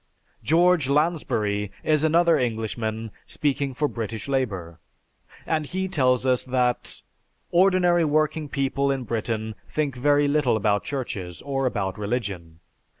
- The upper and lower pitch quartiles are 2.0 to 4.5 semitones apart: No, wide, 5.6 semitones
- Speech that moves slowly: Yes, slow, 125 wpm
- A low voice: Yes, low, 130 Hz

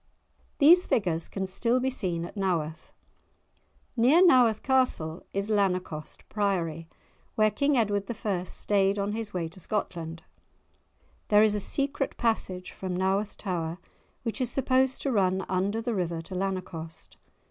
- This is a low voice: No, high, 200 Hz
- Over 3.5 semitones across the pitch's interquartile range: Yes, average, 4.1 semitones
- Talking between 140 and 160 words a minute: Yes, average, 145 wpm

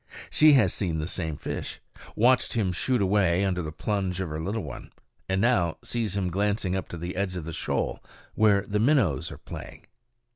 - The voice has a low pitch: Yes, very low, 95 Hz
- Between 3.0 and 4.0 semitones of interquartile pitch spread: Yes, average, 3.5 semitones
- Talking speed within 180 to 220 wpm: Yes, average, 195 wpm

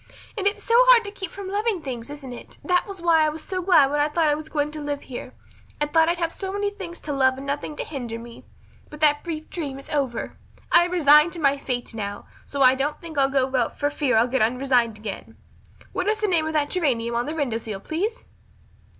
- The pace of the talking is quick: Yes, fast, 250 wpm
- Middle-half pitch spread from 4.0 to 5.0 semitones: Yes, average, 4.7 semitones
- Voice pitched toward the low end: No, very high, 295 Hz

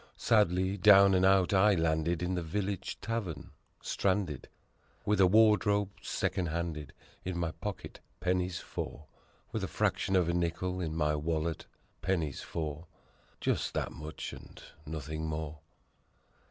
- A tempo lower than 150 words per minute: Yes, average, 140 wpm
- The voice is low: Yes, very low, 90 Hz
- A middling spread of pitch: Yes, average, 3.3 semitones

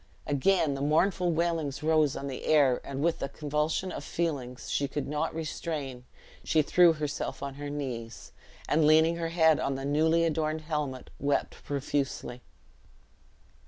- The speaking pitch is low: No, medium, 150 Hz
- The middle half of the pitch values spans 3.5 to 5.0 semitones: No, narrow, 2.5 semitones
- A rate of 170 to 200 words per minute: No, average, 155 wpm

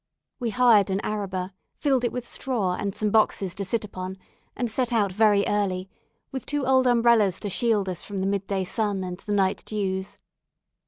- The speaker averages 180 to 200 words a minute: Yes, average, 195 wpm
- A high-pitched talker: Yes, high, 205 Hz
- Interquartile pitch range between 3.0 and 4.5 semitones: Yes, average, 3.5 semitones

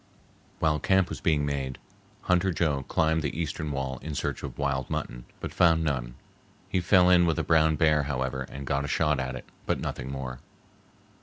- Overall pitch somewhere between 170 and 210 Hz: No, very low, 75 Hz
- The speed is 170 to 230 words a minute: Yes, average, 190 wpm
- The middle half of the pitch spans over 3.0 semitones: Yes, average, 3.4 semitones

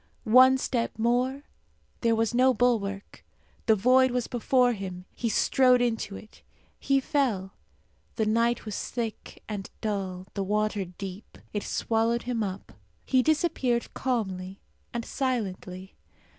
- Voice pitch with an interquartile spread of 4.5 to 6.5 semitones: No, average, 3.9 semitones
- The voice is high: Yes, high, 230 Hz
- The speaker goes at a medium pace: No, slow, 130 wpm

